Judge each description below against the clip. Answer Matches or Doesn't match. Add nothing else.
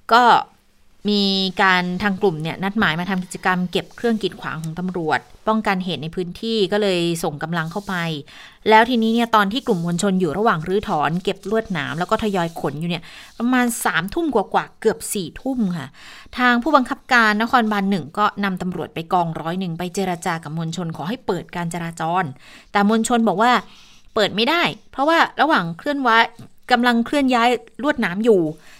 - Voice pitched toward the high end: Matches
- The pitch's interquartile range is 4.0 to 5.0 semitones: Matches